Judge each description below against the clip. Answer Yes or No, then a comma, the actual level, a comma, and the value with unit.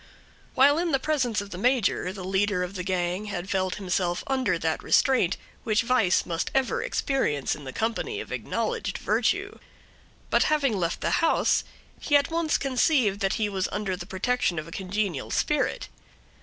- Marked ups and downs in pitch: Yes, wide, 6.4 semitones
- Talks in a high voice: Yes, high, 205 Hz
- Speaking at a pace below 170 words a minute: No, average, 175 wpm